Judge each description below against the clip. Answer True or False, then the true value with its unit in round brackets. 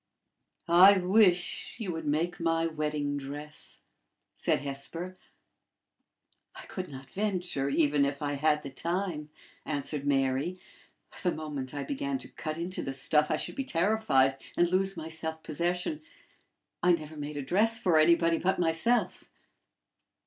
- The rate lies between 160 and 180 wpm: False (145 wpm)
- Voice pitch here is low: False (160 Hz)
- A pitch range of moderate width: True (3.8 semitones)